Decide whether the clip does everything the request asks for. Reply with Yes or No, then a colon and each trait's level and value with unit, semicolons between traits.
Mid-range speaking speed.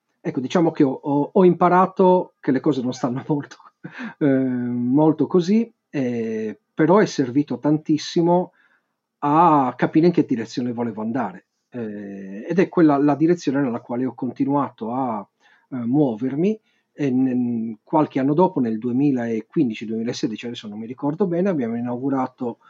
Yes: average, 145 wpm